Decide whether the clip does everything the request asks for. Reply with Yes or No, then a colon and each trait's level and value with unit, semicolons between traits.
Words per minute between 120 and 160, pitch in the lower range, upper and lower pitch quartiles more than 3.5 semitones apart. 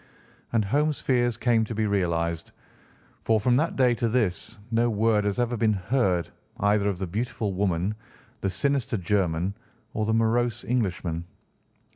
Yes: average, 155 wpm; low, 110 Hz; average, 4.0 semitones